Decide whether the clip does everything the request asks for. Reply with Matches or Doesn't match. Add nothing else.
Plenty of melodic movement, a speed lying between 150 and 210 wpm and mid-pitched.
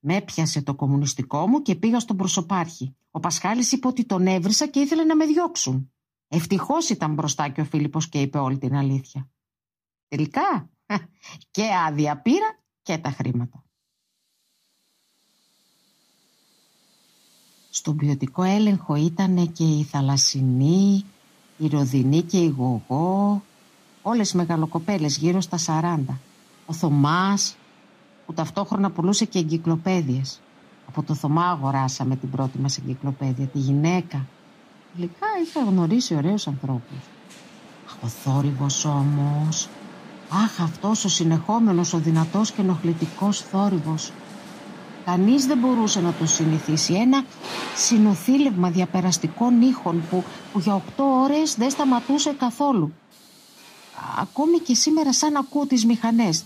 Doesn't match